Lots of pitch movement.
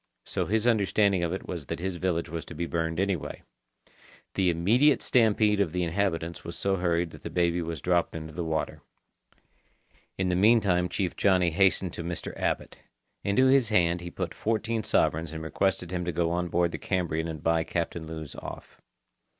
No: average, 2.8 semitones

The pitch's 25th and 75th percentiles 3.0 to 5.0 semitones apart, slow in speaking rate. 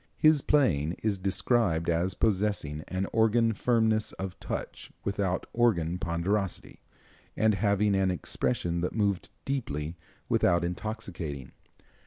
Yes: average, 4.2 semitones; slow, 115 wpm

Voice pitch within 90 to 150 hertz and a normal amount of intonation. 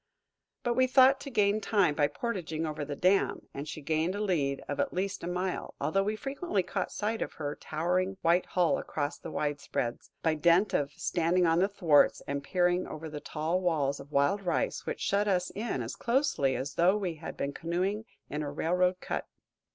No: medium, 175 Hz; average, 4.7 semitones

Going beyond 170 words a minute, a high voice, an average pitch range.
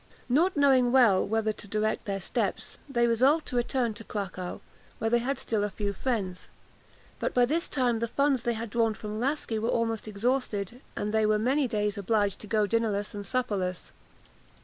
Yes: average, 190 wpm; high, 225 Hz; average, 3.1 semitones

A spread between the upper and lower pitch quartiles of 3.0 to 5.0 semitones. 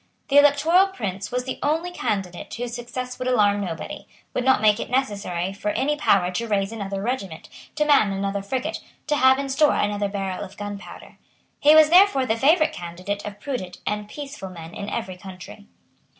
No: wide, 5.6 semitones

